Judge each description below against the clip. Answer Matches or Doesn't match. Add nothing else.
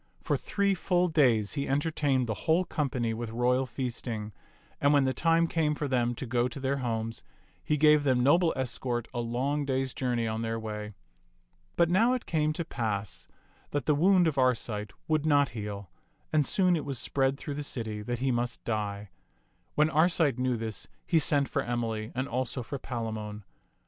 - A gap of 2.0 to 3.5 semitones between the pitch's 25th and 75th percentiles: Doesn't match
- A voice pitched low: Matches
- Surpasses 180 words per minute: Matches